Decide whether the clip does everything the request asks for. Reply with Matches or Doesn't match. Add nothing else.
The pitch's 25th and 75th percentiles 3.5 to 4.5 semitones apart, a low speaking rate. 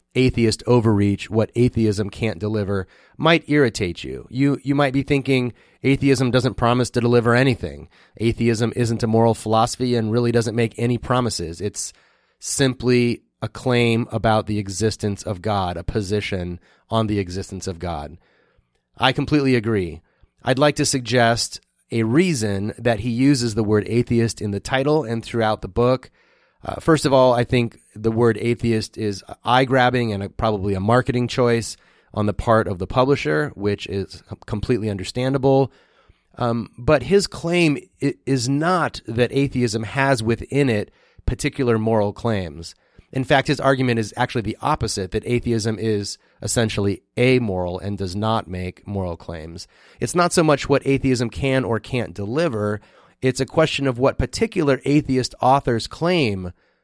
Doesn't match